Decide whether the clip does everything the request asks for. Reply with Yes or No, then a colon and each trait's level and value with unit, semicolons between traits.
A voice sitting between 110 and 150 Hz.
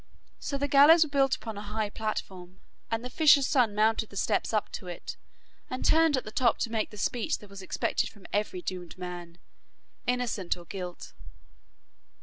No: high, 215 Hz